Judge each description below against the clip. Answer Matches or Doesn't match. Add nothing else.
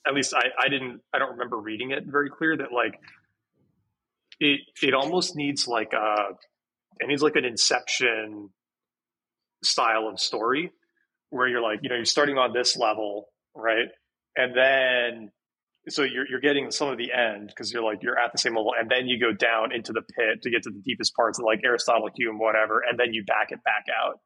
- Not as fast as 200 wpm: Doesn't match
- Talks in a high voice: Doesn't match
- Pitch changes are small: Doesn't match